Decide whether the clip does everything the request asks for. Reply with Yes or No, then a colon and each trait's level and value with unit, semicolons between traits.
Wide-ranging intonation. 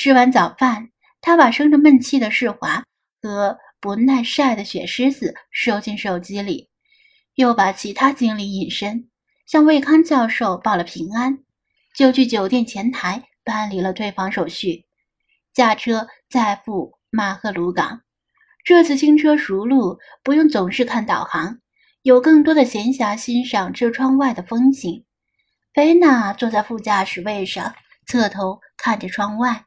No: average, 5.0 semitones